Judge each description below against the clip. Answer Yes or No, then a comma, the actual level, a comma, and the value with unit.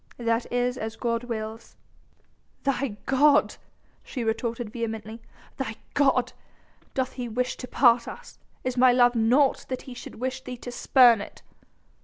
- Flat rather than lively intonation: Yes, narrow, 2.0 semitones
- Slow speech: No, average, 150 wpm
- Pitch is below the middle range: No, high, 245 Hz